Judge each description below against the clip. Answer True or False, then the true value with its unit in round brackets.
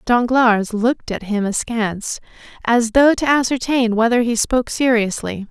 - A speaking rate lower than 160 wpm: True (140 wpm)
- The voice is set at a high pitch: True (235 Hz)